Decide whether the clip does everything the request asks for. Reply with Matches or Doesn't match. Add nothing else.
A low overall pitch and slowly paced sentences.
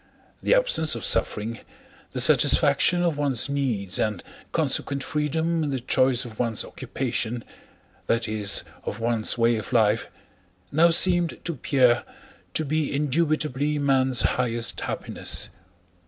Matches